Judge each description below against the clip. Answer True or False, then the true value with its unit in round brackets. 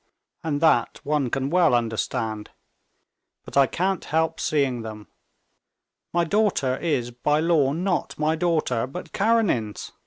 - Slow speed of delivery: True (130 wpm)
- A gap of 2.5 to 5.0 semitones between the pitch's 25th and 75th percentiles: False (5.5 semitones)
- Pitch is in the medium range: True (150 Hz)